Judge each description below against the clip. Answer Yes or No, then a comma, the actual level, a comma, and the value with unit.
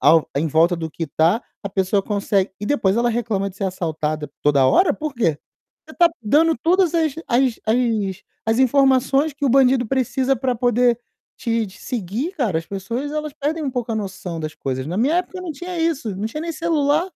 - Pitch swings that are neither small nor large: No, wide, 7.0 semitones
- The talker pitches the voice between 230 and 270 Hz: Yes, high, 235 Hz